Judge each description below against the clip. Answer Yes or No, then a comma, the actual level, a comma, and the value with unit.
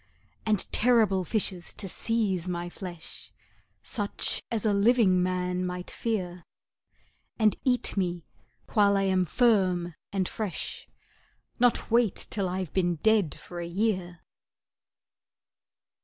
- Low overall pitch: No, high, 190 Hz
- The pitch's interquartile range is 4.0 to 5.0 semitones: No, average, 3.3 semitones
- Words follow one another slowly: Yes, slow, 120 wpm